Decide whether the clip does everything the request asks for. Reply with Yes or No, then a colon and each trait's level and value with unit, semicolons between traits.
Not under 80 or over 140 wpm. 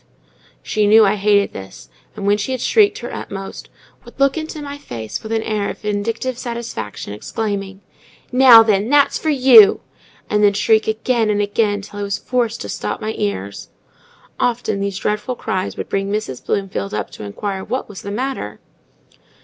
No: average, 175 wpm